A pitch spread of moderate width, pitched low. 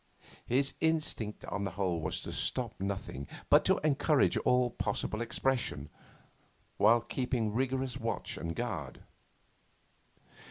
Yes: average, 4.8 semitones; low, 115 Hz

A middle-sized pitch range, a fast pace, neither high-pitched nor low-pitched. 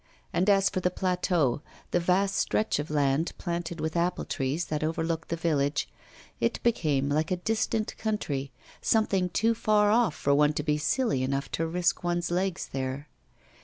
No: average, 4.3 semitones; average, 170 wpm; medium, 170 Hz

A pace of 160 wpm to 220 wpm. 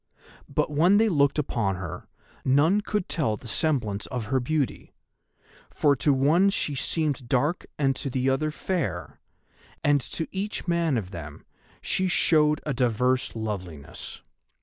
No: average, 150 wpm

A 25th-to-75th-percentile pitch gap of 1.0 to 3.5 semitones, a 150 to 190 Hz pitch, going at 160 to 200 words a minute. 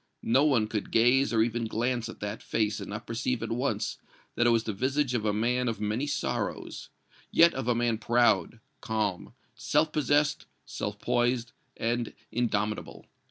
No: narrow, 2.4 semitones; low, 120 Hz; average, 170 wpm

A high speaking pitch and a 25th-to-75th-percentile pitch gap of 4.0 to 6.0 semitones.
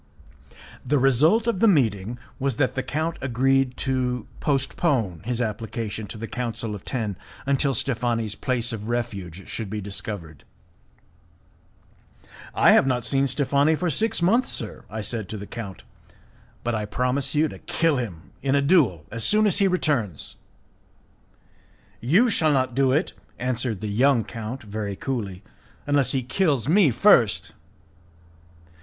No: low, 125 Hz; average, 4.4 semitones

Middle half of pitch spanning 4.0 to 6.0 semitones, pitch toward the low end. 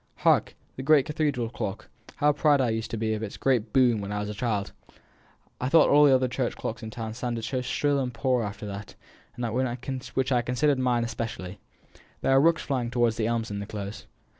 No: average, 3.2 semitones; low, 120 Hz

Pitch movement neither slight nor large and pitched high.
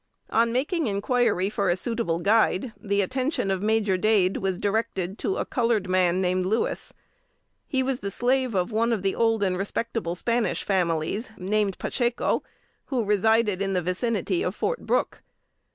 Yes: average, 3.8 semitones; high, 210 Hz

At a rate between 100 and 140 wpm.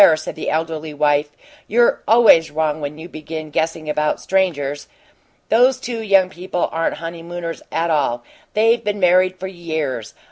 No: average, 150 wpm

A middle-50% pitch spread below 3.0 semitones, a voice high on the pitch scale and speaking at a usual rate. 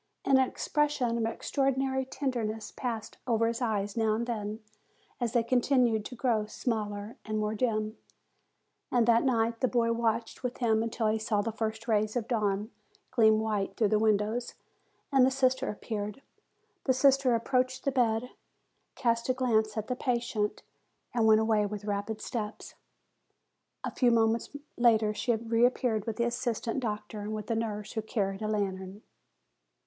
Yes: narrow, 2.4 semitones; high, 225 Hz; average, 170 wpm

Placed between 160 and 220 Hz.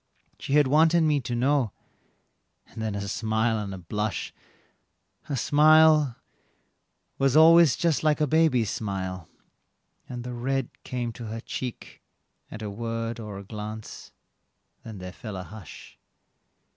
No: low, 120 Hz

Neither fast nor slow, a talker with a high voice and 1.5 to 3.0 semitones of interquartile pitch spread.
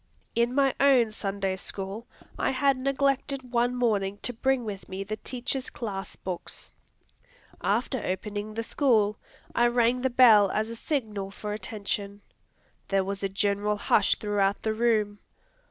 No: average, 150 wpm; high, 215 Hz; average, 3.7 semitones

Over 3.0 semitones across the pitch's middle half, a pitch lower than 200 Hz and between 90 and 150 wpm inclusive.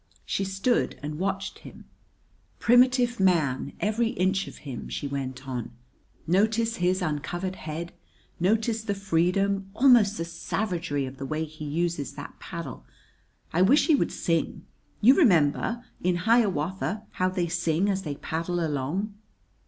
Yes: average, 5.1 semitones; medium, 185 Hz; average, 145 wpm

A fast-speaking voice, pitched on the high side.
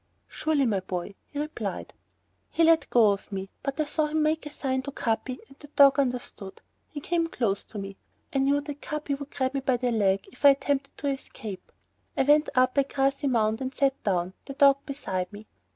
Yes: fast, 215 wpm; very high, 270 Hz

